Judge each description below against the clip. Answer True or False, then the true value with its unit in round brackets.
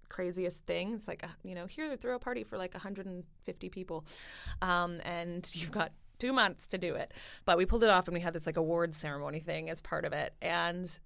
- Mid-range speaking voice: True (175 Hz)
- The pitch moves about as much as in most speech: False (2.1 semitones)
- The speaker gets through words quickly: True (220 wpm)